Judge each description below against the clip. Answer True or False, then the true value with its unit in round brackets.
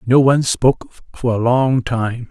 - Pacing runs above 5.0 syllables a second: False (4.6 syllables/s)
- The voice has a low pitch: True (125 Hz)